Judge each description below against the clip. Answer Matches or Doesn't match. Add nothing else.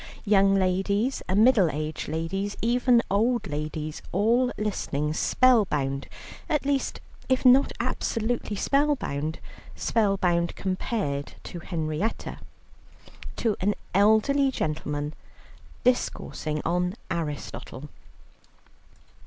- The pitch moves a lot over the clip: Matches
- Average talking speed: Doesn't match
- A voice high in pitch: Matches